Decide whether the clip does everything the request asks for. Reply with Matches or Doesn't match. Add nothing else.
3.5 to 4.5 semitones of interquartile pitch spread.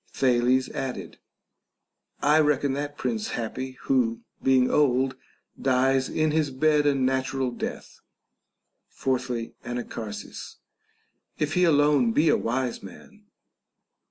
Doesn't match